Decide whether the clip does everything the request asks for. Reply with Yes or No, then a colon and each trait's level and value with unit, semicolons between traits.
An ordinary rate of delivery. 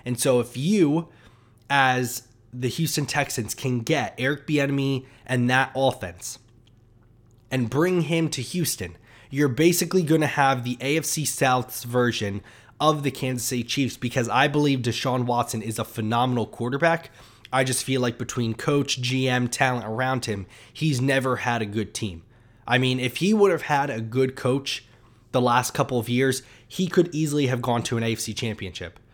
Yes: average, 170 wpm